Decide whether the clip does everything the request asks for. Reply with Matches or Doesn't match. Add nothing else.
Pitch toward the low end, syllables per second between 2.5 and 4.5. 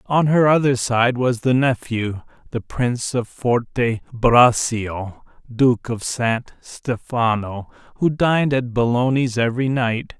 Matches